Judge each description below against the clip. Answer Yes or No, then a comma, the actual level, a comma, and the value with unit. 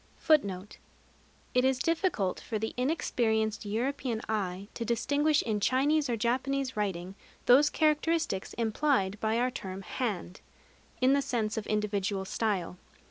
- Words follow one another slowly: Yes, slow, 130 wpm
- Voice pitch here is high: Yes, high, 230 Hz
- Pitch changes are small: No, average, 4.6 semitones